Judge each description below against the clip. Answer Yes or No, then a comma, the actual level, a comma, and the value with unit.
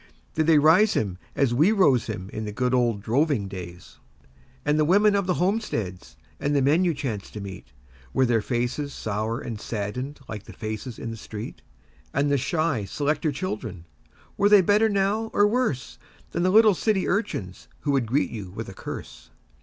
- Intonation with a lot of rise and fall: Yes, wide, 8.4 semitones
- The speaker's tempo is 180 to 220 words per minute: Yes, average, 190 wpm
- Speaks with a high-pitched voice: No, low, 135 Hz